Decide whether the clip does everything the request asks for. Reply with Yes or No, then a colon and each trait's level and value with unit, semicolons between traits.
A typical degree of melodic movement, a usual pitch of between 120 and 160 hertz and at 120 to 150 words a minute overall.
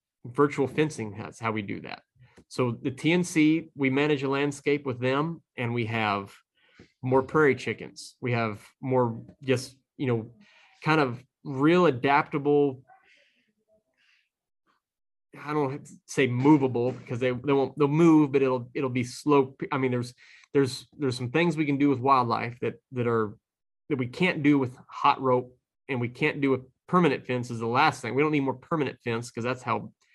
No: average, 3.1 semitones; low, 135 Hz; average, 175 wpm